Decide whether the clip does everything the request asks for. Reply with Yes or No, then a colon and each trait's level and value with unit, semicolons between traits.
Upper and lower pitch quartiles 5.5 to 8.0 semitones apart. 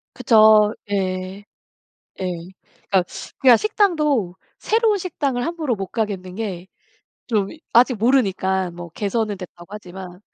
No: average, 5.1 semitones